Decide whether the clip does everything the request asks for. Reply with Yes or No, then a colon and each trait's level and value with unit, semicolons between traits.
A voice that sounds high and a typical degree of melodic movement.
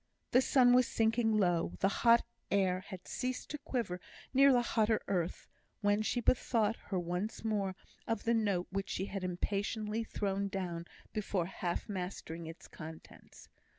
Yes: high, 205 Hz; average, 3.9 semitones